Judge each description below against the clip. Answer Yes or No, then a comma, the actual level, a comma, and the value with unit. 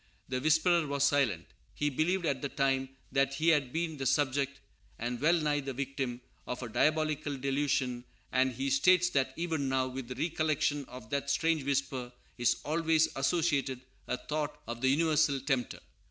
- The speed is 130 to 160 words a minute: No, average, 170 wpm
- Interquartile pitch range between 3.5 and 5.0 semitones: No, average, 3.0 semitones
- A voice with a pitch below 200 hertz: Yes, medium, 140 Hz